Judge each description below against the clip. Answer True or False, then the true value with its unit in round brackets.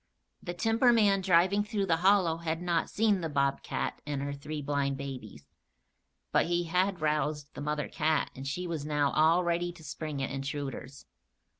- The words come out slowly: False (170 wpm)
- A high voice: False (160 Hz)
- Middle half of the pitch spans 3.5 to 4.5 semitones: True (3.9 semitones)